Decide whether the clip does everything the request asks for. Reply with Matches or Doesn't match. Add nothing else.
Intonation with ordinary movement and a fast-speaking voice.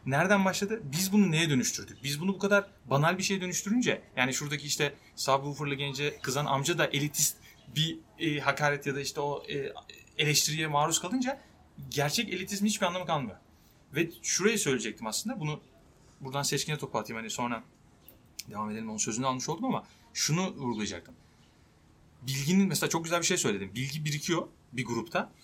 Matches